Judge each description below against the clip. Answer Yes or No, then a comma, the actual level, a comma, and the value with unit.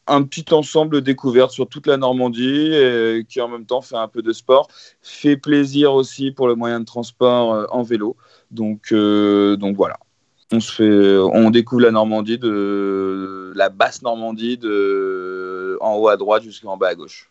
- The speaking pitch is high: No, low, 115 Hz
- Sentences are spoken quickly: No, average, 180 wpm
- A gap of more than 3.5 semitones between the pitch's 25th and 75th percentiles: Yes, average, 3.9 semitones